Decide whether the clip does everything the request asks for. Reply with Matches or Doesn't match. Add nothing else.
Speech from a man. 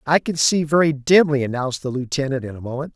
Matches